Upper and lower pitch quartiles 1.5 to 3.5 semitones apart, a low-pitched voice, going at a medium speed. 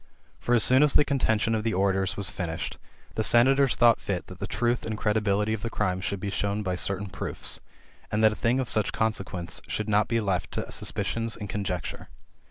No: average, 2.8 semitones; low, 105 Hz; fast, 220 wpm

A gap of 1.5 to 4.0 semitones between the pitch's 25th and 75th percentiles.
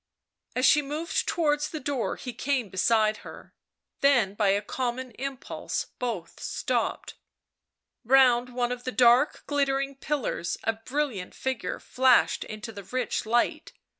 Yes: average, 3.6 semitones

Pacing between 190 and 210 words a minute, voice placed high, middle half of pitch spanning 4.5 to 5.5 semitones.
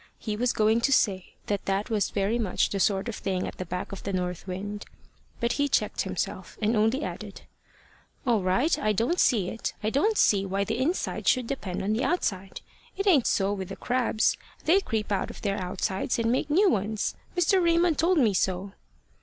Yes: fast, 205 wpm; high, 215 Hz; average, 4.9 semitones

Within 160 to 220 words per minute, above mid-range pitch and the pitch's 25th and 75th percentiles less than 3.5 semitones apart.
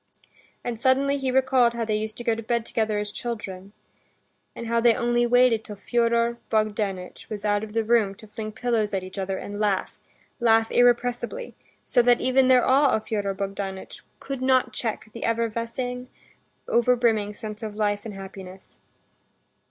Yes: average, 170 wpm; high, 225 Hz; narrow, 2.6 semitones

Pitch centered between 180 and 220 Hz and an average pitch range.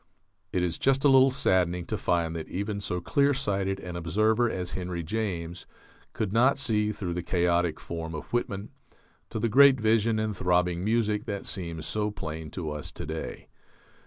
No: very low, 95 Hz; average, 4.2 semitones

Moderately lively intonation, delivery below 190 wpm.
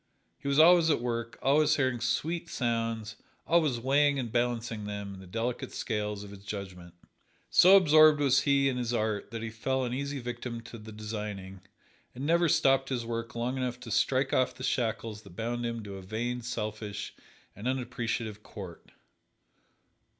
Yes: average, 3.7 semitones; average, 175 wpm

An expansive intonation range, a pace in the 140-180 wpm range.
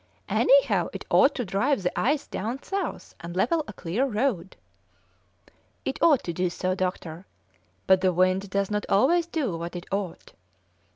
Yes: wide, 6.9 semitones; average, 165 wpm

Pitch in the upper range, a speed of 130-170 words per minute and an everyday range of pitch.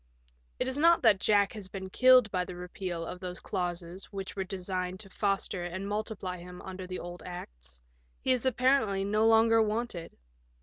No: high, 195 Hz; average, 180 wpm; average, 3.4 semitones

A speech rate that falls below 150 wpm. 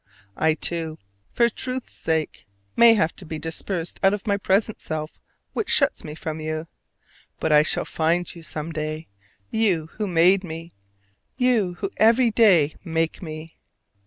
No: average, 160 wpm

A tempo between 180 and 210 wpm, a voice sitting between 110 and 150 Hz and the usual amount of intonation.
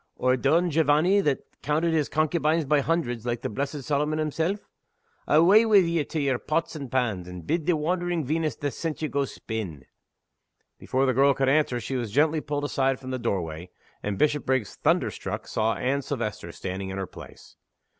Yes: average, 185 wpm; medium, 140 Hz; average, 4.5 semitones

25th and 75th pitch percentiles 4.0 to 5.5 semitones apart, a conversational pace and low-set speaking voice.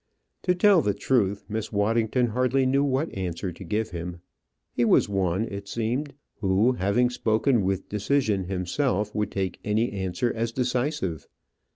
Yes: average, 4.5 semitones; average, 155 wpm; low, 110 Hz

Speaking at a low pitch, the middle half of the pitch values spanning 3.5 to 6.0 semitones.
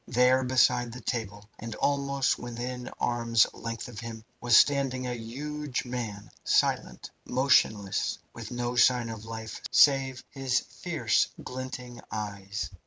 No: low, 120 Hz; narrow, 2.4 semitones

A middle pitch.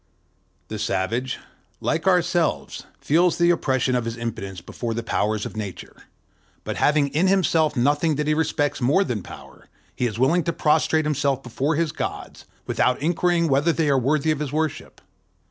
Yes: medium, 145 Hz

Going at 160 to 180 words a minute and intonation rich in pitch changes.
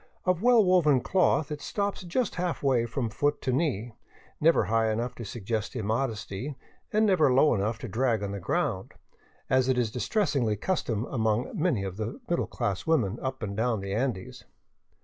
Yes: average, 175 wpm; wide, 6.2 semitones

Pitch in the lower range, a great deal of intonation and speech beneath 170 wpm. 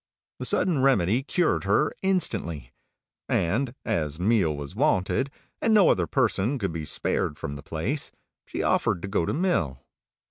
Yes: low, 100 Hz; wide, 8.9 semitones; average, 155 wpm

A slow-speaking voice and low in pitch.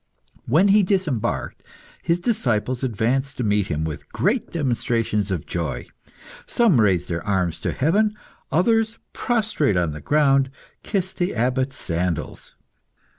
Yes: slow, 130 wpm; low, 130 Hz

